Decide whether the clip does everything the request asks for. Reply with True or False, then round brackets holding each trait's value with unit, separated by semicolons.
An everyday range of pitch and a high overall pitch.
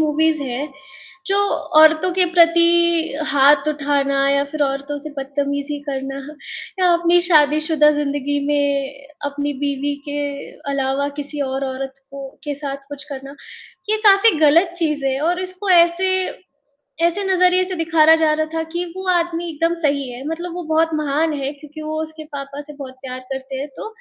True (3.1 semitones; 295 Hz)